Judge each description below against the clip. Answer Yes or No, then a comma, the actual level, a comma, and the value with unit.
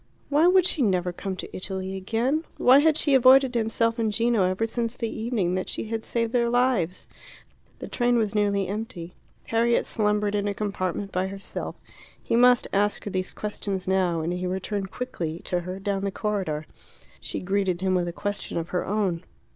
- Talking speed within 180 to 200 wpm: Yes, average, 190 wpm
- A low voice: No, high, 205 Hz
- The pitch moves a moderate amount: Yes, average, 3.8 semitones